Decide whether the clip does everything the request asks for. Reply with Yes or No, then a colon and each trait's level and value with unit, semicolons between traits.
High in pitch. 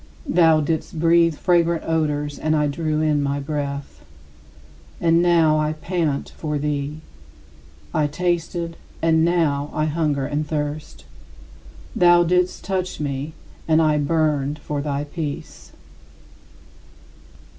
No: medium, 155 Hz